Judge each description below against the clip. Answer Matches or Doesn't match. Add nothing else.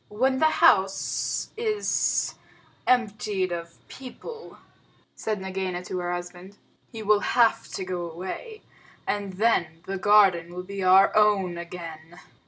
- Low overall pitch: Doesn't match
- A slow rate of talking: Matches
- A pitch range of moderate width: Matches